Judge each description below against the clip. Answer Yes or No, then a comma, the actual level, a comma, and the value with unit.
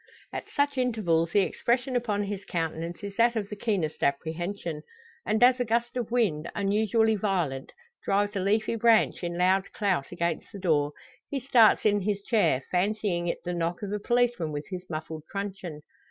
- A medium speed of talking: Yes, average, 180 wpm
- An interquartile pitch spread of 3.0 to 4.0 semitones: No, average, 4.4 semitones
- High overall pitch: Yes, high, 200 Hz